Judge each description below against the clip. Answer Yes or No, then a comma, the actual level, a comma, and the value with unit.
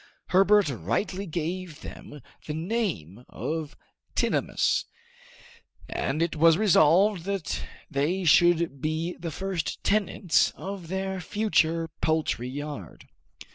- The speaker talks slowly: Yes, slow, 105 wpm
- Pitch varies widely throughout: No, average, 3.9 semitones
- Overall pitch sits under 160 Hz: No, medium, 165 Hz